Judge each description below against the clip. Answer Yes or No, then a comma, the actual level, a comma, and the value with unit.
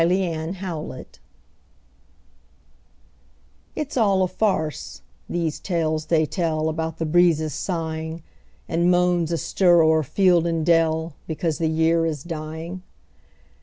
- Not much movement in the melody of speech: Yes, narrow, 1.8 semitones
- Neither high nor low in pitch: Yes, medium, 165 Hz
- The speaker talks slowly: Yes, slow, 115 wpm